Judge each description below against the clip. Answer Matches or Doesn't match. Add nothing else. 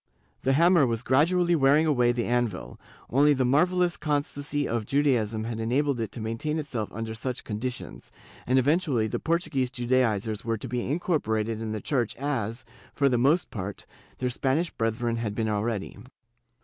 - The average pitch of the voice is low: Matches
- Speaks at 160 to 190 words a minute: Matches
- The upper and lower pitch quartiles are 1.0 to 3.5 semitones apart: Doesn't match